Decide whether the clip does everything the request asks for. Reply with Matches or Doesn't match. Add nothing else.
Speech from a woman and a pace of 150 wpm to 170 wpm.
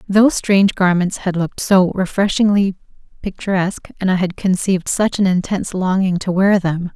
Matches